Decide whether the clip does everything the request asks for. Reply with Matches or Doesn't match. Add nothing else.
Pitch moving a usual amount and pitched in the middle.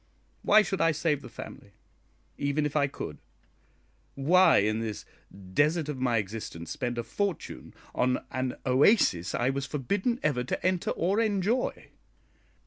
Doesn't match